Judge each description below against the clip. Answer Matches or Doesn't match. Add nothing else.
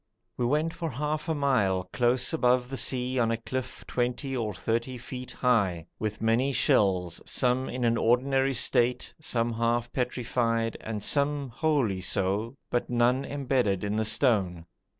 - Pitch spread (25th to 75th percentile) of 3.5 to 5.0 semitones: Doesn't match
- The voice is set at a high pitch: Doesn't match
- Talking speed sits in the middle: Matches